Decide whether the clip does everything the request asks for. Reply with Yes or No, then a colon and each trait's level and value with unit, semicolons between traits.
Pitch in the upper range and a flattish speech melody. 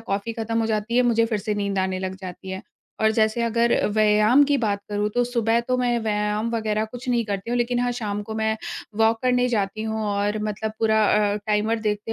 Yes: high, 220 Hz; narrow, 2.0 semitones